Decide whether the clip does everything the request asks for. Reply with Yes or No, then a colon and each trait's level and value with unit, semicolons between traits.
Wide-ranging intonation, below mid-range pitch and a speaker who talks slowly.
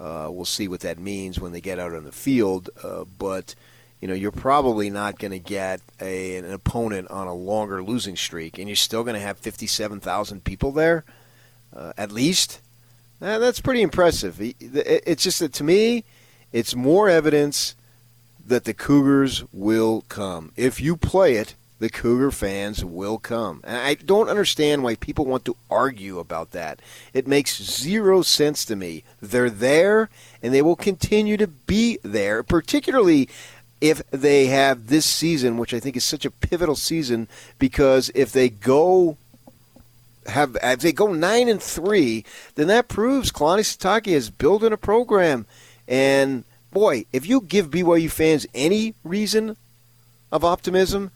No: wide, 7.2 semitones; low, 125 Hz; average, 165 wpm